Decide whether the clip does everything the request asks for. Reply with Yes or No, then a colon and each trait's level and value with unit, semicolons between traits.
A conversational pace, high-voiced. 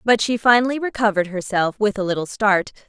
Yes: average, 190 wpm; high, 210 Hz